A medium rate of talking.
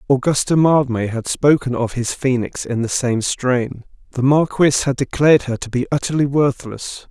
Yes: average, 170 wpm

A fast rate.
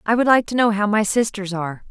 Yes: fast, 285 wpm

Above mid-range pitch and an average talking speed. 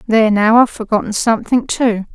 Yes: high, 225 Hz; average, 170 wpm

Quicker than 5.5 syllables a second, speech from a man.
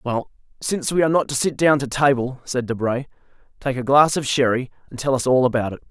Yes: 6.2 syllables/s; male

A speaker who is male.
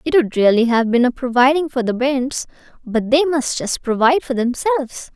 No: female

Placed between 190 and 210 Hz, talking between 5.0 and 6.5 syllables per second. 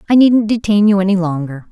Yes: high, 200 Hz; 6.0 syllables/s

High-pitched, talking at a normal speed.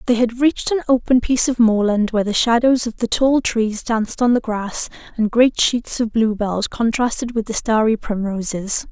Yes: high, 230 Hz; average, 190 wpm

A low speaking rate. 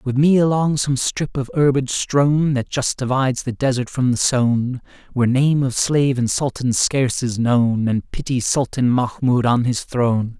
No: average, 185 wpm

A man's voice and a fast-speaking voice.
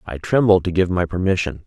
Yes: male; fast, 215 wpm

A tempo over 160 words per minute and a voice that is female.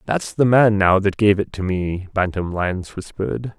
No: average, 200 wpm; male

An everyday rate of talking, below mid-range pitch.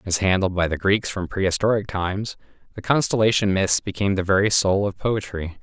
Yes: average, 180 wpm; low, 100 Hz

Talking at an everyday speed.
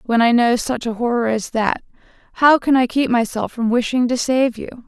No: fast, 220 wpm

